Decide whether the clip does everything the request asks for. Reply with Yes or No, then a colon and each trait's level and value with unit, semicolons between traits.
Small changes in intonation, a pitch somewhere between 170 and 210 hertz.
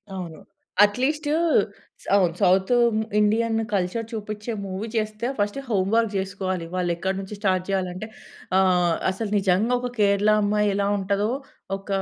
Yes: narrow, 2.2 semitones; high, 200 Hz